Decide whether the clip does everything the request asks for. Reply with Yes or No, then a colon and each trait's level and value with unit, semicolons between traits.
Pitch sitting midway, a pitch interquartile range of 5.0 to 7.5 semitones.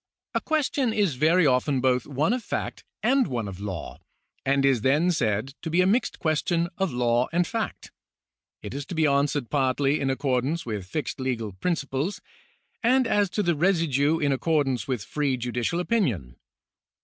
Yes: medium, 145 Hz; wide, 5.5 semitones